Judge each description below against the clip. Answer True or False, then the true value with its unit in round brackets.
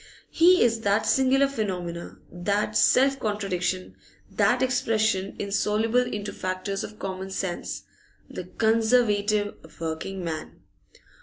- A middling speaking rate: False (105 wpm)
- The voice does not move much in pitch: False (3.4 semitones)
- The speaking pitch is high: True (205 Hz)